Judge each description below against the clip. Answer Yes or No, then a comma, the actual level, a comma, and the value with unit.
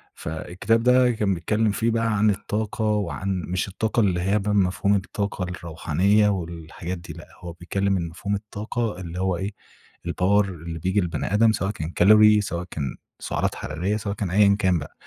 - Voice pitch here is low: Yes, low, 100 Hz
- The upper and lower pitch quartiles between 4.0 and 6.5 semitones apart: No, average, 3.3 semitones